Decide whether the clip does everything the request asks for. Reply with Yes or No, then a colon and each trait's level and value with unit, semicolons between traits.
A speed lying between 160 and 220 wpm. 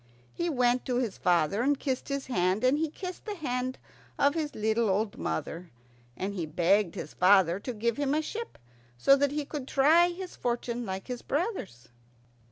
Yes: average, 185 wpm